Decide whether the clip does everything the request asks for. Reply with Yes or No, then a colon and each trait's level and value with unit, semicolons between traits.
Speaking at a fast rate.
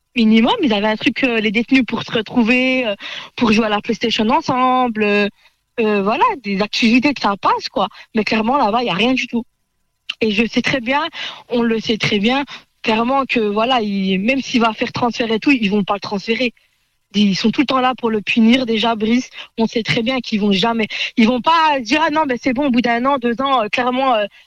Yes: fast, 240 wpm